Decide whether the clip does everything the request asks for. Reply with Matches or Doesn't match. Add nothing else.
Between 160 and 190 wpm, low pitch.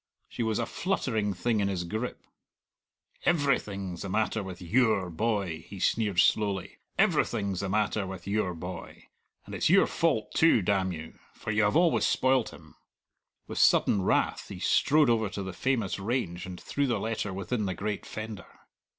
Matches